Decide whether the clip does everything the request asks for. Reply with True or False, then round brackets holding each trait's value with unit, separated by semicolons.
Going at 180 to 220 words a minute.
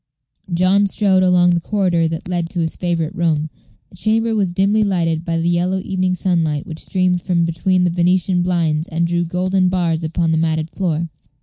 True (190 wpm)